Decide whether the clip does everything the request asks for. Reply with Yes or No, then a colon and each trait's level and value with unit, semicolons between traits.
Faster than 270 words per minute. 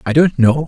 No: fast, 265 wpm